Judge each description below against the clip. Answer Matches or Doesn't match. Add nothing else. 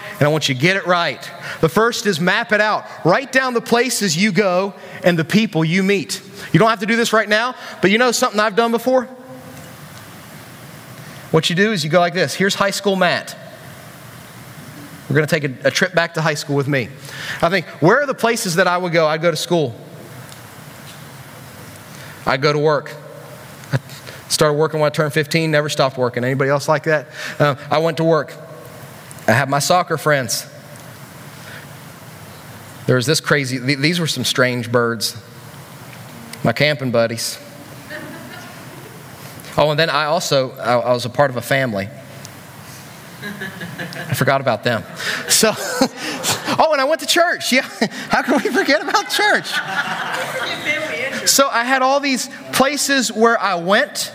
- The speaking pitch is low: Doesn't match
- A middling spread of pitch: Doesn't match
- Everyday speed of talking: Matches